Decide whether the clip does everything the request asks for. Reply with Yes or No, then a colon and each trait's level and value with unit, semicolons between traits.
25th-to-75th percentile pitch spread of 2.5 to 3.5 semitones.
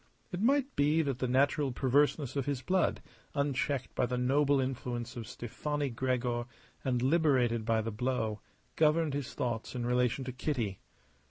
Yes: average, 2.9 semitones